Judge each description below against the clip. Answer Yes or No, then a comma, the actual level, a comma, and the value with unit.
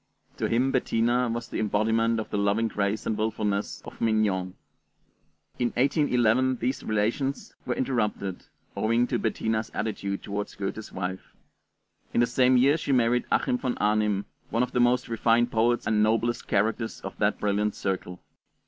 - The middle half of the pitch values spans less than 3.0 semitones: Yes, narrow, 2.6 semitones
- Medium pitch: No, low, 115 Hz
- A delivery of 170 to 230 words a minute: No, average, 155 wpm